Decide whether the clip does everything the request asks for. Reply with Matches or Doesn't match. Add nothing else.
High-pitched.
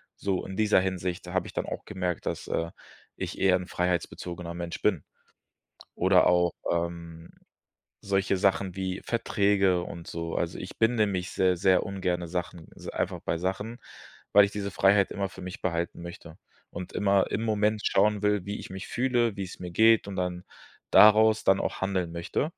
Doesn't match